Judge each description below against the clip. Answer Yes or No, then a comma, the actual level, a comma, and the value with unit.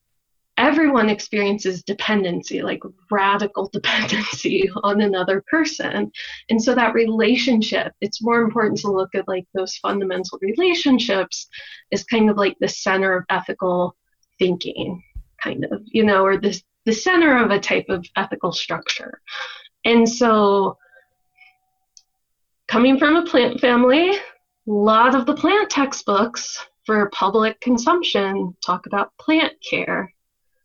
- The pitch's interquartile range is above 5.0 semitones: Yes, wide, 5.5 semitones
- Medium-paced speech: No, slow, 130 wpm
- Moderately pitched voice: No, high, 220 Hz